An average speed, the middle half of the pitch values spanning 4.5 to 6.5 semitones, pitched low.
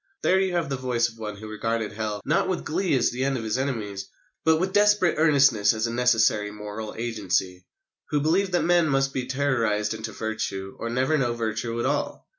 No: fast, 210 wpm; average, 4.8 semitones; low, 120 Hz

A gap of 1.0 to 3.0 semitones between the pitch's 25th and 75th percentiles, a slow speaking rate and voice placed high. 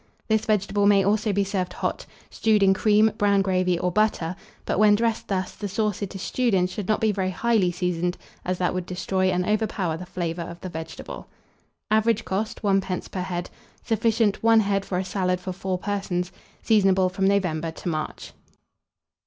No: narrow, 2.6 semitones; average, 185 wpm; high, 195 Hz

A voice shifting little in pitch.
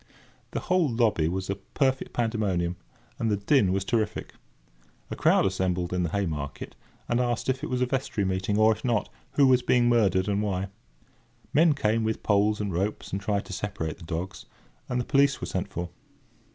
No: average, 4.4 semitones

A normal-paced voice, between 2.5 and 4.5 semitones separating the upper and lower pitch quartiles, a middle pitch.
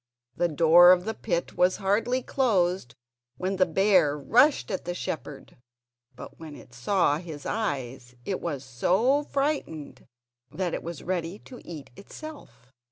No: average, 150 wpm; wide, 5.6 semitones; medium, 175 Hz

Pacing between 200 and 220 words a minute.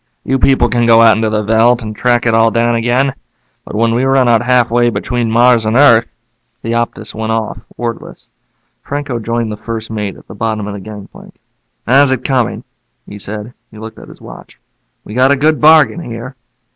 Yes: fast, 205 wpm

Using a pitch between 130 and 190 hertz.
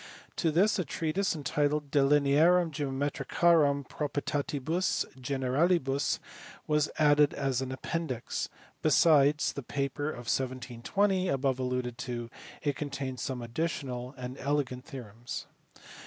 Yes: medium, 140 Hz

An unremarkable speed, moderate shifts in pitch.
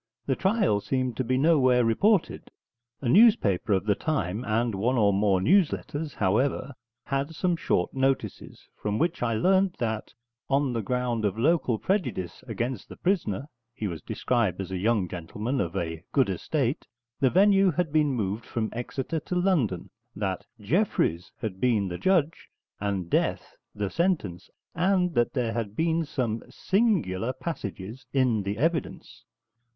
No: average, 155 wpm; wide, 7.7 semitones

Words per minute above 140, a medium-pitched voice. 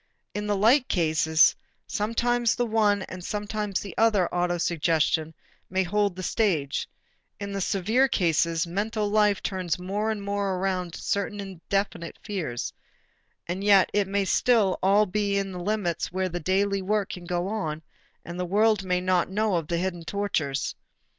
No: average, 160 wpm; high, 195 Hz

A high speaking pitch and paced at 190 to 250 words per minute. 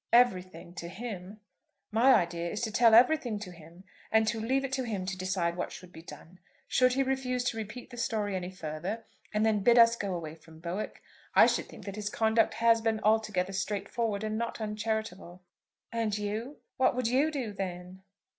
Yes: high, 215 Hz; average, 195 wpm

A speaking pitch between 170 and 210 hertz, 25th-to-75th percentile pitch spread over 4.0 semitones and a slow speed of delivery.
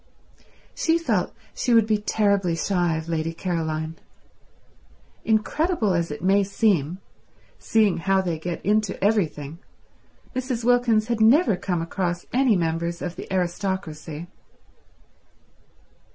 Yes: high, 190 Hz; average, 4.7 semitones; slow, 120 wpm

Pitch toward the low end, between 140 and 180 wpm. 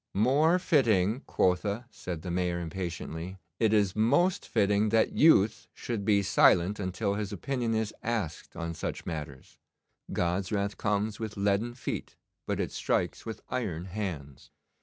Yes: low, 100 Hz; average, 145 wpm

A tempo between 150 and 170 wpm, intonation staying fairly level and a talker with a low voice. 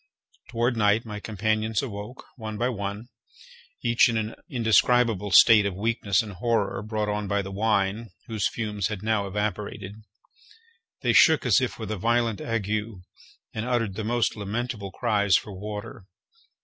Yes: average, 155 wpm; narrow, 2.1 semitones; low, 110 Hz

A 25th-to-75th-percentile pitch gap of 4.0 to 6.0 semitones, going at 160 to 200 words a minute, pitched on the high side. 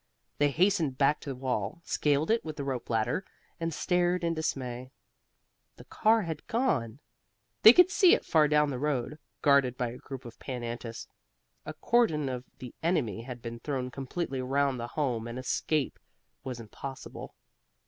No: average, 4.3 semitones; average, 170 wpm; medium, 140 Hz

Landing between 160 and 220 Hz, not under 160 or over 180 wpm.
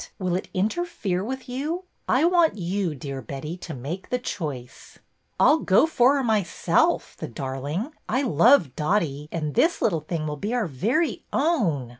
Yes: medium, 185 Hz; average, 170 wpm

